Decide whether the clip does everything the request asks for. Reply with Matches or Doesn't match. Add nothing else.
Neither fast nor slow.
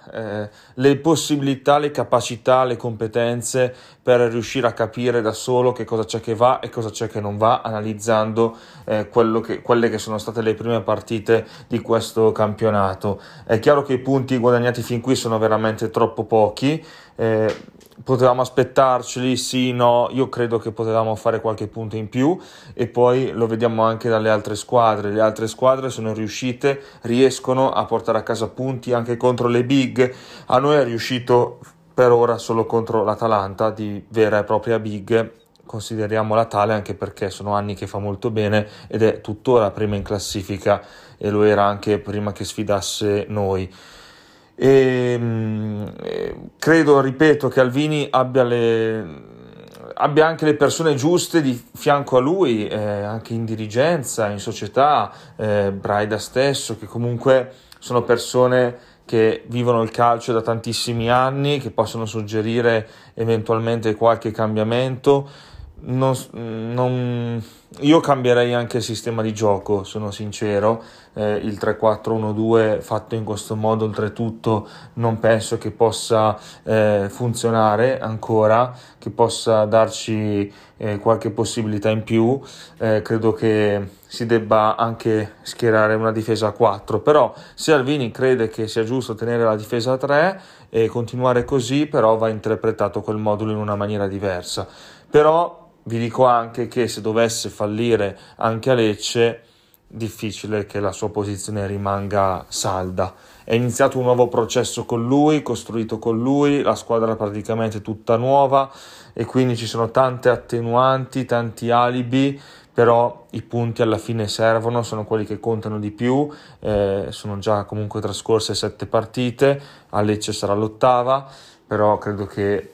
Matches